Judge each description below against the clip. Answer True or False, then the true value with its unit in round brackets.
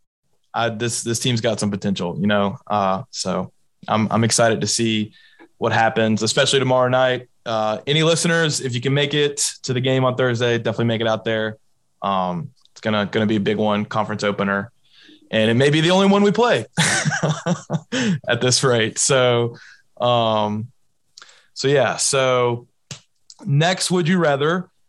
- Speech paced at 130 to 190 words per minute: True (170 wpm)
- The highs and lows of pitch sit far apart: False (4.8 semitones)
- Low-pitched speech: True (120 Hz)